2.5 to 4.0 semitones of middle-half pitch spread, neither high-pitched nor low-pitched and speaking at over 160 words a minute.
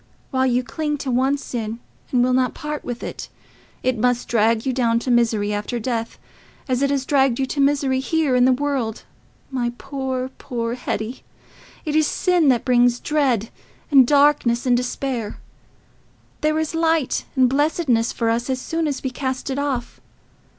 No: average, 2.9 semitones; very high, 255 Hz; average, 175 wpm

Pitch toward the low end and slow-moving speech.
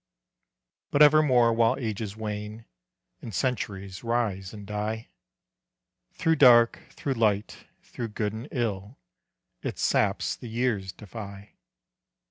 Yes: low, 110 Hz; slow, 110 wpm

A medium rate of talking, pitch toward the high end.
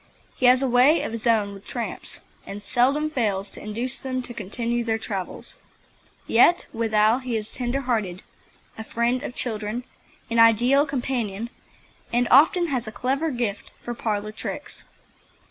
Yes: average, 160 wpm; high, 235 Hz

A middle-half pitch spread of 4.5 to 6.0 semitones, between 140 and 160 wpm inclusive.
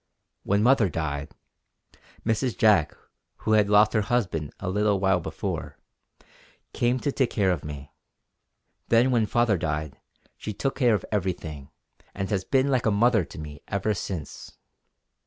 Yes: wide, 5.4 semitones; average, 155 wpm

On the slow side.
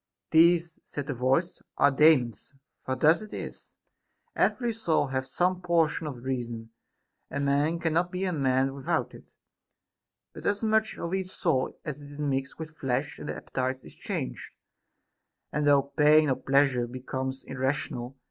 No: average, 155 wpm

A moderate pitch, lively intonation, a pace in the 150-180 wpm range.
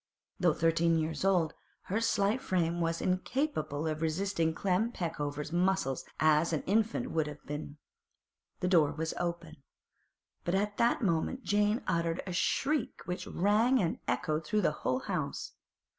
No: medium, 175 Hz; average, 4.1 semitones; average, 155 wpm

